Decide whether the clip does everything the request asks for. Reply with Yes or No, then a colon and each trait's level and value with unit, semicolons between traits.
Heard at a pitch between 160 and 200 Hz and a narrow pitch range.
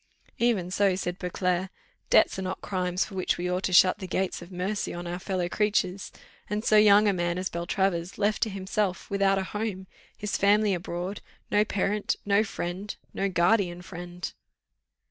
Yes: high, 190 Hz; narrow, 2.2 semitones